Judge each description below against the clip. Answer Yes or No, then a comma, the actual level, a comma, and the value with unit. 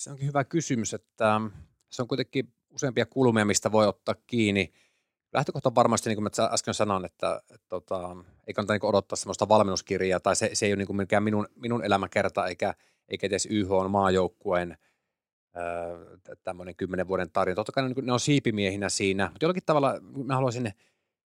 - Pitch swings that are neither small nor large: Yes, average, 4.2 semitones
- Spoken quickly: Yes, fast, 185 wpm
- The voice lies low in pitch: Yes, low, 105 Hz